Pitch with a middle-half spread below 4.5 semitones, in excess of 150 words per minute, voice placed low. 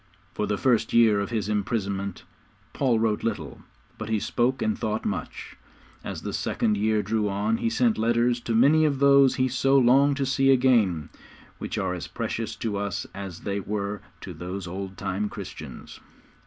Yes: average, 3.8 semitones; average, 180 wpm; low, 110 Hz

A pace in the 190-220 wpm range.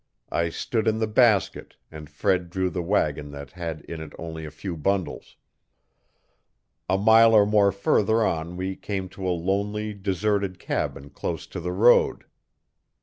No: average, 160 wpm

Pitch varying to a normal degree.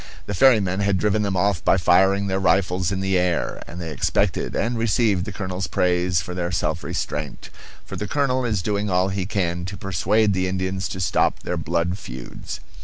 No: narrow, 2.2 semitones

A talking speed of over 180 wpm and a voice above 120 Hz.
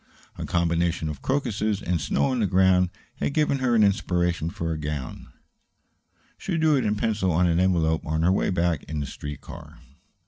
No: average, 195 wpm; very low, 90 Hz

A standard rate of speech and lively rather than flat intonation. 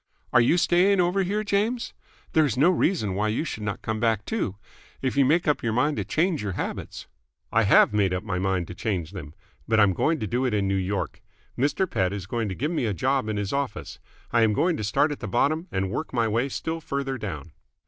No: fast, 245 wpm; wide, 7.7 semitones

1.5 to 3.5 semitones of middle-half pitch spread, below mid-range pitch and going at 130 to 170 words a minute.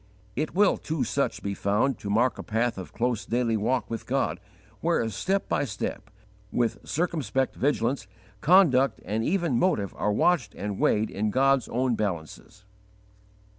No: average, 4.7 semitones; low, 120 Hz; average, 155 wpm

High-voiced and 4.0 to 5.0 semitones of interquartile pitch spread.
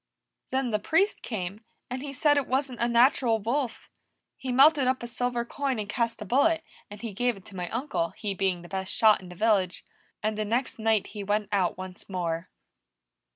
Yes: high, 225 Hz; average, 4.6 semitones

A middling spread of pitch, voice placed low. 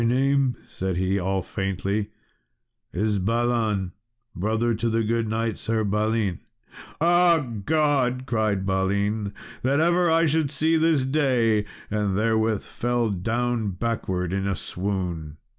Yes: average, 4.3 semitones; low, 110 Hz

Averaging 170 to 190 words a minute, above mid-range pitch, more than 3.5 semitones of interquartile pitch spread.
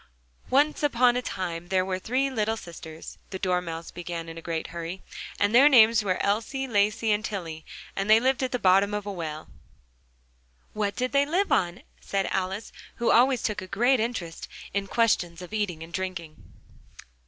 Yes: average, 185 wpm; high, 200 Hz; average, 5.2 semitones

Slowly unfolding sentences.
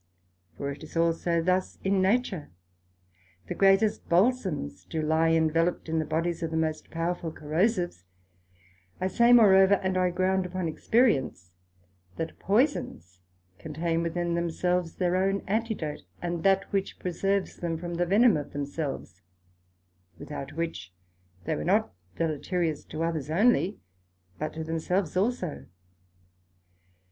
Yes: slow, 130 wpm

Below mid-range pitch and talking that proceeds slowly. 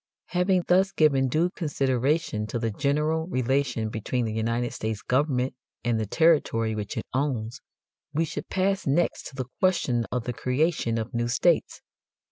No: low, 130 Hz; average, 160 wpm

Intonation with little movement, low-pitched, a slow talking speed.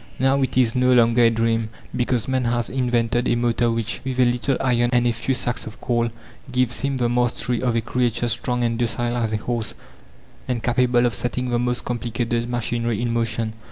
No: narrow, 1.1 semitones; low, 120 Hz; fast, 205 wpm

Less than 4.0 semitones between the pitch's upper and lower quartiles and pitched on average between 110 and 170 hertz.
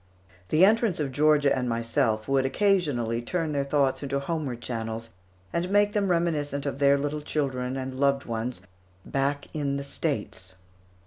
Yes: average, 3.3 semitones; medium, 140 Hz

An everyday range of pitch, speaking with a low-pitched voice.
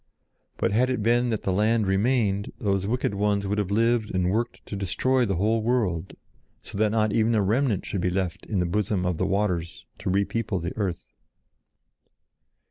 Yes: average, 3.0 semitones; low, 105 Hz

